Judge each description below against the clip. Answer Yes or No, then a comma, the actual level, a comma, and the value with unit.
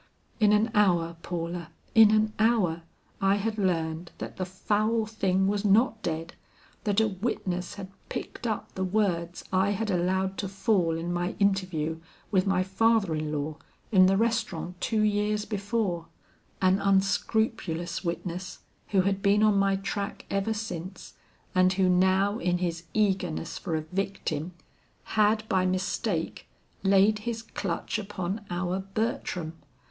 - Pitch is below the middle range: No, high, 195 Hz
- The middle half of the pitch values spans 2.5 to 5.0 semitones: Yes, average, 3.0 semitones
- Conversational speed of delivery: Yes, average, 145 wpm